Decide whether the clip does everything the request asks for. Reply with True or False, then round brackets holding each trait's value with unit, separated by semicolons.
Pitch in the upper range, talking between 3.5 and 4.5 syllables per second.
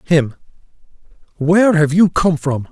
False (160 Hz; 4.4 syllables/s)